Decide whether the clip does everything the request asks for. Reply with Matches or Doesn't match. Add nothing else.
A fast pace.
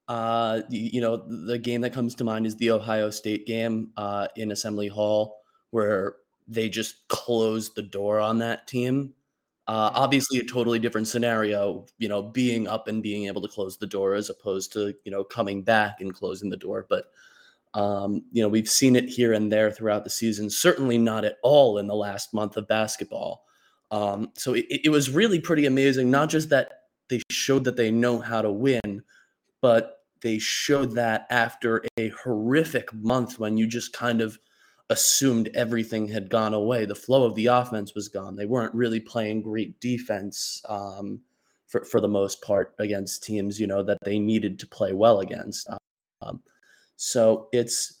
Doesn't match